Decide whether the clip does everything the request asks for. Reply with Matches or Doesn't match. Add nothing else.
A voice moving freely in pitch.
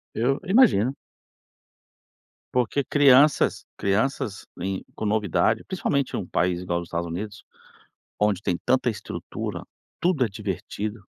Matches